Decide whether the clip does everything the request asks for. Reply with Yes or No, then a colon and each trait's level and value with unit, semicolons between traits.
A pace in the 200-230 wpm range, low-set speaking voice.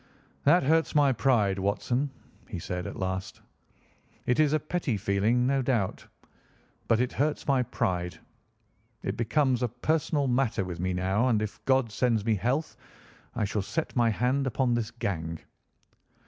No: average, 160 wpm; low, 120 Hz